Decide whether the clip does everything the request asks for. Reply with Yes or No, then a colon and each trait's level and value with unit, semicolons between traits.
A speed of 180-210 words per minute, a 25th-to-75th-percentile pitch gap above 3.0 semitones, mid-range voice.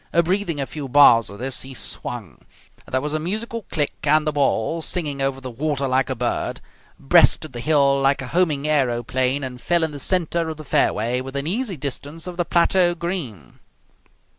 Yes: average, 190 wpm; average, 4.1 semitones; medium, 145 Hz